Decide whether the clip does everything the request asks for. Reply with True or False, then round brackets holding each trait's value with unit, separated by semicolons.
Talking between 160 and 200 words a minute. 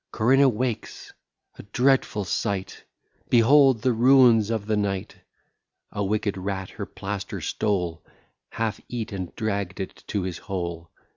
False (135 wpm)